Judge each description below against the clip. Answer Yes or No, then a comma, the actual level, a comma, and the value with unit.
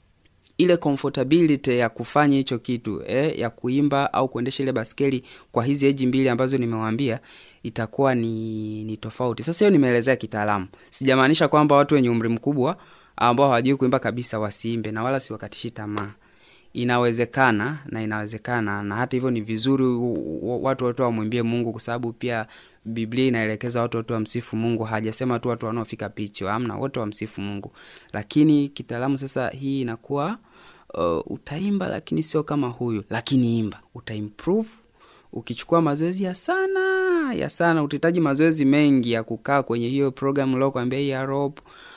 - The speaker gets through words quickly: Yes, fast, 145 wpm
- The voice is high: No, low, 125 Hz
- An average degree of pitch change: Yes, average, 3.7 semitones